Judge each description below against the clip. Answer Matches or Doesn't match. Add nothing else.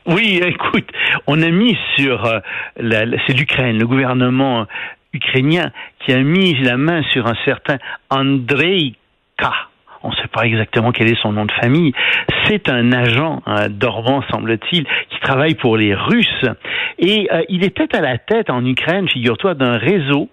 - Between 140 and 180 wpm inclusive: Matches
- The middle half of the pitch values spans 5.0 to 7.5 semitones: Matches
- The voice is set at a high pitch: Doesn't match